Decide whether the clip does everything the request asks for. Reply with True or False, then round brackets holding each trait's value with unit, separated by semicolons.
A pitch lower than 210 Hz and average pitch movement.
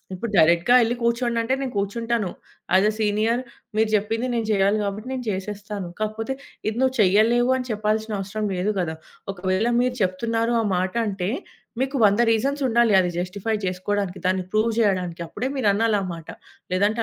False (215 Hz; 3.3 semitones)